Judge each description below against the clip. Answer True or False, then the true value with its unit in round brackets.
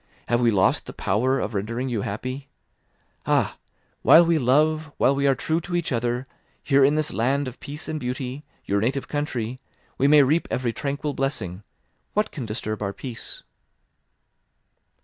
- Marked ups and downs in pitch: False (3.8 semitones)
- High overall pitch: False (130 Hz)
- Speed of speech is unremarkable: True (165 wpm)